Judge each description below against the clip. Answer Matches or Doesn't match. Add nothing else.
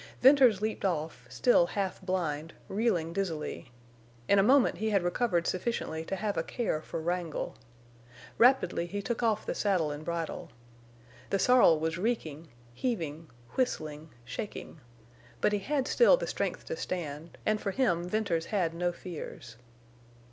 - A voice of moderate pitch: Matches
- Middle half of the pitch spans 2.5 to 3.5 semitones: Doesn't match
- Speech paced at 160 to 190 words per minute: Doesn't match